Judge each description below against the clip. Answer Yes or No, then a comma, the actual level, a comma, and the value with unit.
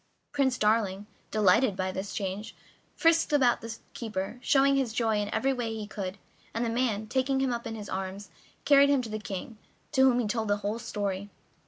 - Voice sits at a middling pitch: No, high, 225 Hz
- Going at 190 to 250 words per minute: Yes, average, 200 wpm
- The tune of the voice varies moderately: Yes, average, 3.9 semitones